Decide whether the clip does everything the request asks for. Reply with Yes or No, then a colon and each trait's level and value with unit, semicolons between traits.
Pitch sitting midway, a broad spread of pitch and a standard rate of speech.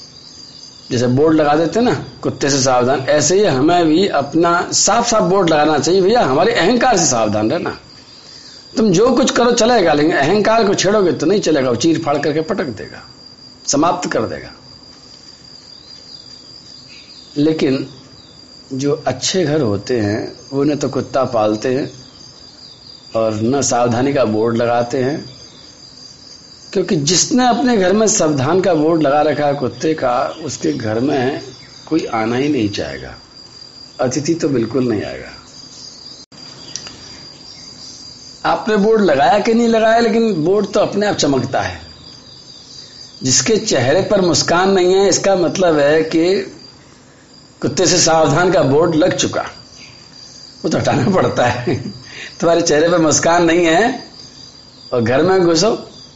Yes: medium, 155 Hz; wide, 6.4 semitones; average, 145 wpm